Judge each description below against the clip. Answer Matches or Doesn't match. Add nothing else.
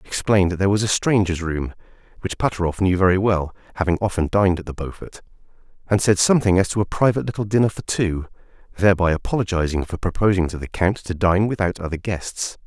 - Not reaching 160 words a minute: Doesn't match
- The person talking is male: Matches